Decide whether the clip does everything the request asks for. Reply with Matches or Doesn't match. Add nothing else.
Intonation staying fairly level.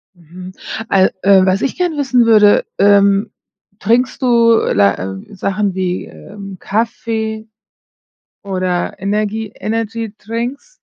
Doesn't match